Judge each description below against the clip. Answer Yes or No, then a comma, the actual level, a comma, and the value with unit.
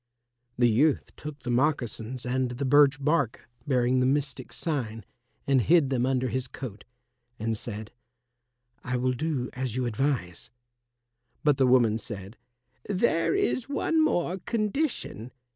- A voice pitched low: Yes, low, 130 Hz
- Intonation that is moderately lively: Yes, average, 3.6 semitones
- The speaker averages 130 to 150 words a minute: Yes, average, 140 wpm